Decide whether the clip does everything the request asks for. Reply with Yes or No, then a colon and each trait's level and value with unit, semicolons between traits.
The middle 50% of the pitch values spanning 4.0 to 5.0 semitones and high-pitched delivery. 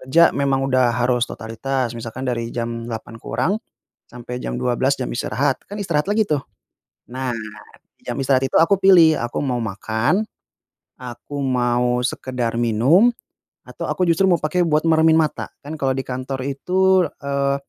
No: average, 4.7 semitones; low, 130 Hz